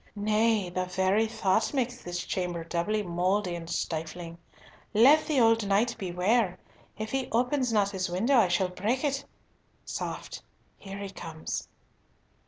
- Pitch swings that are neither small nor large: Yes, average, 4.3 semitones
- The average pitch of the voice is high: Yes, high, 200 Hz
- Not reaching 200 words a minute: Yes, average, 145 wpm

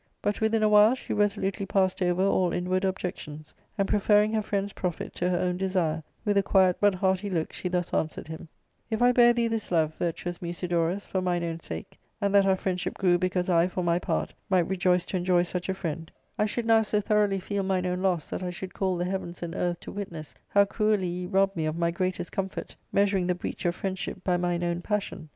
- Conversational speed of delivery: No, fast, 235 wpm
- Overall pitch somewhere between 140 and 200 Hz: Yes, medium, 185 Hz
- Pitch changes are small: Yes, narrow, 2.2 semitones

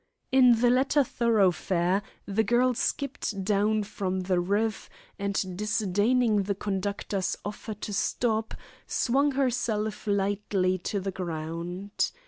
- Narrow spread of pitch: No, average, 3.2 semitones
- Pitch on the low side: No, high, 205 Hz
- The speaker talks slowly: Yes, slow, 115 wpm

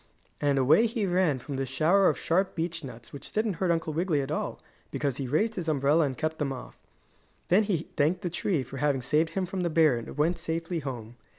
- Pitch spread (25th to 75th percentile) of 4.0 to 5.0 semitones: Yes, average, 4.4 semitones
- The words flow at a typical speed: No, fast, 225 wpm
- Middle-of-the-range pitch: Yes, medium, 160 Hz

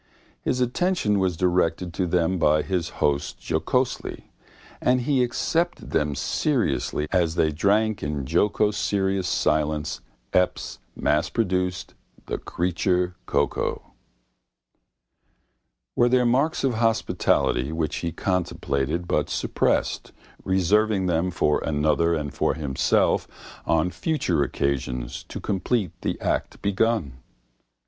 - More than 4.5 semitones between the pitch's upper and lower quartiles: Yes, wide, 5.6 semitones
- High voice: No, very low, 90 Hz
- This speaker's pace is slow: Yes, slow, 110 wpm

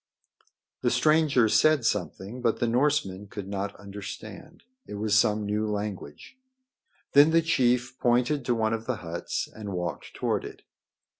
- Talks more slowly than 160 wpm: Yes, average, 150 wpm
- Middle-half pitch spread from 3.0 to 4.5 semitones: Yes, average, 3.9 semitones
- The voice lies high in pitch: No, low, 110 Hz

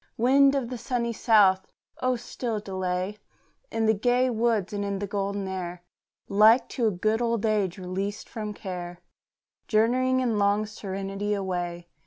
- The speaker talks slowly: No, average, 155 wpm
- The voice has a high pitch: Yes, high, 210 Hz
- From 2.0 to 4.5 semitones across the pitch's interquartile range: Yes, average, 3.4 semitones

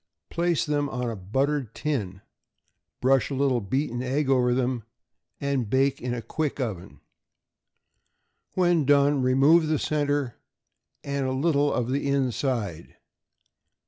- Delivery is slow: Yes, slow, 130 wpm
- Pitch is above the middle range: No, low, 135 Hz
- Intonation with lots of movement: No, average, 2.8 semitones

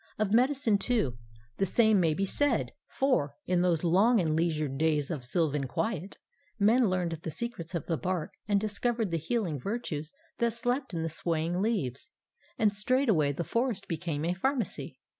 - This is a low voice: No, medium, 185 Hz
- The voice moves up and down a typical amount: No, wide, 6.2 semitones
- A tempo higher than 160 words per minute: Yes, average, 170 wpm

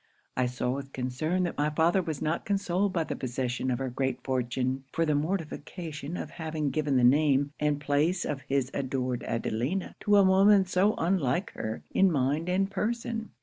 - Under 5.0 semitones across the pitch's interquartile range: No, wide, 5.6 semitones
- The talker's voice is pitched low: No, medium, 150 Hz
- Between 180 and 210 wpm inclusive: Yes, average, 185 wpm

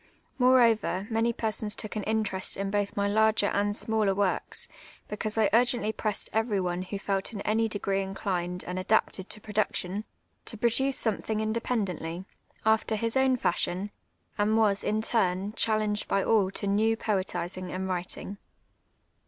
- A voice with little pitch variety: Yes, narrow, 2.3 semitones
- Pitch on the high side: Yes, high, 210 Hz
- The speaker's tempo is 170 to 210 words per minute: No, average, 160 wpm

